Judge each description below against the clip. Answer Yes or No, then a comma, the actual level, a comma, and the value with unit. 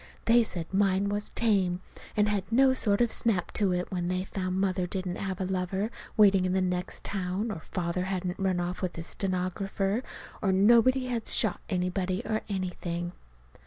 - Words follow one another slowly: No, average, 180 wpm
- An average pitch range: No, narrow, 2.3 semitones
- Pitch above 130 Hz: Yes, high, 190 Hz